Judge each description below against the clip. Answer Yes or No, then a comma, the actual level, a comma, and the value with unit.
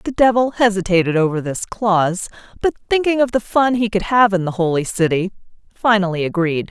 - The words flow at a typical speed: Yes, average, 180 wpm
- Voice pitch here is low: No, high, 200 Hz